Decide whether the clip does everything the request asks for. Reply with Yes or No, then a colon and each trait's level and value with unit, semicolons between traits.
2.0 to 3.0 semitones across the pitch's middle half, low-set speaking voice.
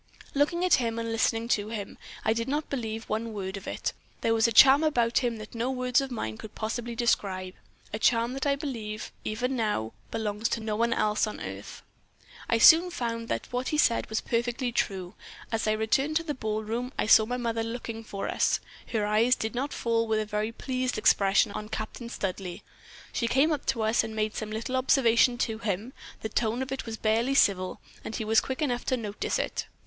No: narrow, 2.5 semitones; high, 230 Hz